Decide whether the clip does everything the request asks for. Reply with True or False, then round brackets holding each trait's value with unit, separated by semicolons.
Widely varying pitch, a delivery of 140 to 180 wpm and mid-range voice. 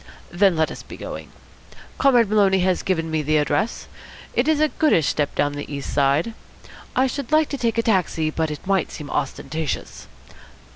False (7.3 semitones; 190 wpm; 180 Hz)